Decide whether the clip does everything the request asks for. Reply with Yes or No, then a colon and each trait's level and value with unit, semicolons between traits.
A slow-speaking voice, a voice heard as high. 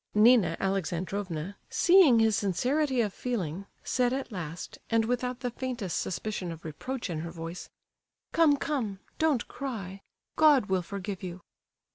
Yes: slow, 125 wpm; high, 210 Hz